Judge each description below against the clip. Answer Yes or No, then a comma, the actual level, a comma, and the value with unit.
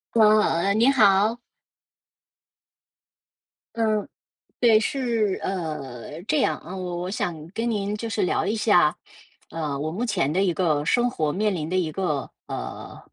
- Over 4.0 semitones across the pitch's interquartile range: Yes, average, 5.3 semitones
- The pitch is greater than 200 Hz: No, high, 195 Hz